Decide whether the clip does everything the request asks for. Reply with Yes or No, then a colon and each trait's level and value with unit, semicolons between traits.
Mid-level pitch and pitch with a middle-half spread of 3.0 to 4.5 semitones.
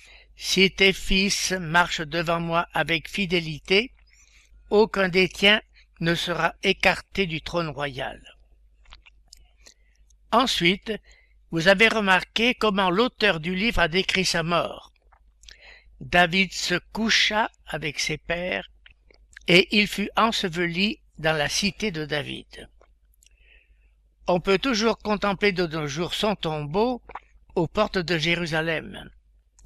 Yes: medium, 180 Hz; average, 4.2 semitones